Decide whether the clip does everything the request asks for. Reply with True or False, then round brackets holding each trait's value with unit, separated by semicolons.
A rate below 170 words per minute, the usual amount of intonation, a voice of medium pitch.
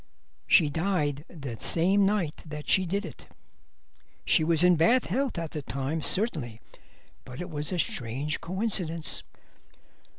True (140 wpm; 4.2 semitones; 165 Hz)